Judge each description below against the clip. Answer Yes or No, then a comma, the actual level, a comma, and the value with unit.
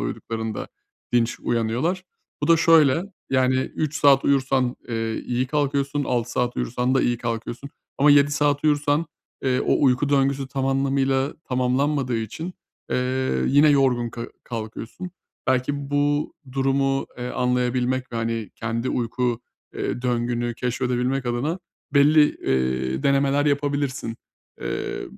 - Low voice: Yes, low, 130 Hz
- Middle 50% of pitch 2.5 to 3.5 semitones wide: Yes, average, 2.8 semitones